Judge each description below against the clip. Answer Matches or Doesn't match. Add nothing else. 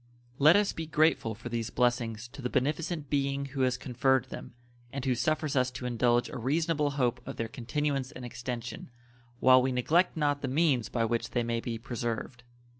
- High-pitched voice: Doesn't match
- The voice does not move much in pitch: Doesn't match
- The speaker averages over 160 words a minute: Matches